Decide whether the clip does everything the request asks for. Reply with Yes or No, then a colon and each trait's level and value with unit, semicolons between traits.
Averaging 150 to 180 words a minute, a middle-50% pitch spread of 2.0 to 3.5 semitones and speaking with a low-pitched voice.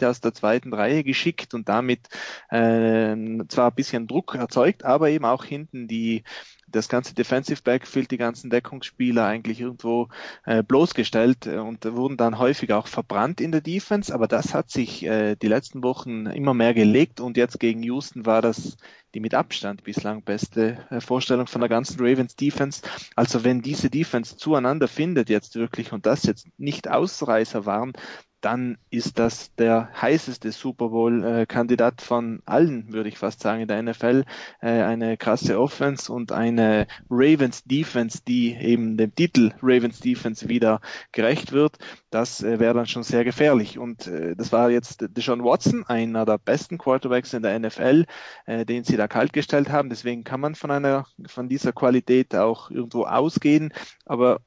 Yes: average, 160 wpm; narrow, 2.4 semitones; low, 120 Hz